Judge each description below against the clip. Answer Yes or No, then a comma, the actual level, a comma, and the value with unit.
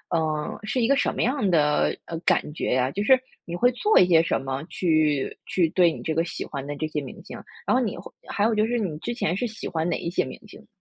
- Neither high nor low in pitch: Yes, medium, 170 Hz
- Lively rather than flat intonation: Yes, wide, 6.0 semitones